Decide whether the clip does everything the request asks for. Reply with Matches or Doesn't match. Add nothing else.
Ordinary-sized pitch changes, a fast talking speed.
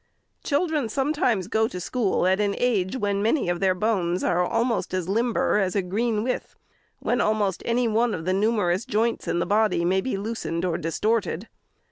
Doesn't match